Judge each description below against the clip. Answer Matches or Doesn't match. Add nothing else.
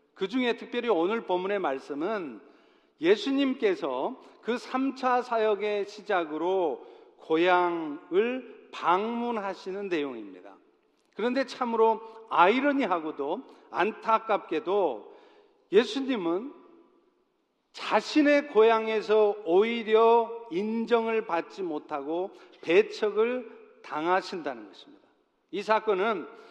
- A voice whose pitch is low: Doesn't match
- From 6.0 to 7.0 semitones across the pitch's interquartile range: Matches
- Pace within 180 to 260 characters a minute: Matches